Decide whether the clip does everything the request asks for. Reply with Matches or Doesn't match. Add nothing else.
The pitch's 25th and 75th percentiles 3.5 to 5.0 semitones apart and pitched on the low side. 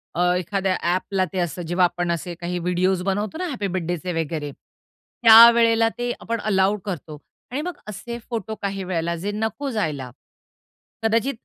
Doesn't match